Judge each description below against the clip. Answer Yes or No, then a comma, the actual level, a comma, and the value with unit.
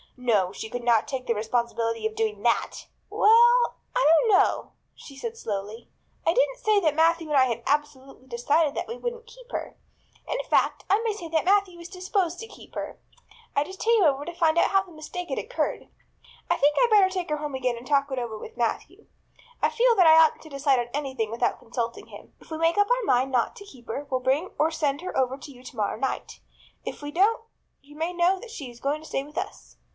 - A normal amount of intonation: No, wide, 7.1 semitones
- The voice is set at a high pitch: Yes, very high, 300 Hz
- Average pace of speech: No, fast, 230 wpm